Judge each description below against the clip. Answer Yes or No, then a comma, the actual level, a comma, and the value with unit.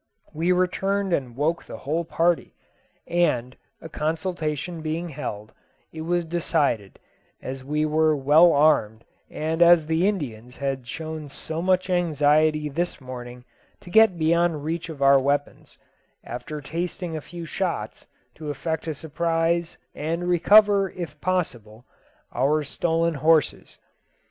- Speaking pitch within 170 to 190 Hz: No, medium, 160 Hz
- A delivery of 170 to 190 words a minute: No, slow, 135 wpm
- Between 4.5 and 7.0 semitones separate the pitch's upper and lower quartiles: No, average, 3.2 semitones